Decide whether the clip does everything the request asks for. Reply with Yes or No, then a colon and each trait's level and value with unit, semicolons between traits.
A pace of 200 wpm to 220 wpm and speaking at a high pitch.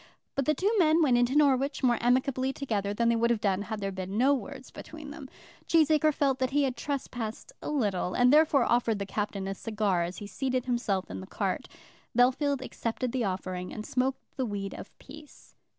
Yes: fast, 205 wpm; very high, 250 Hz